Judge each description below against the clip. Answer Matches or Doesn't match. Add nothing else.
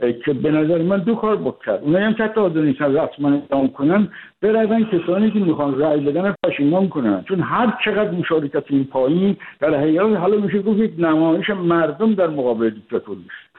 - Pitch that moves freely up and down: Matches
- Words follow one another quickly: Matches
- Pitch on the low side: Doesn't match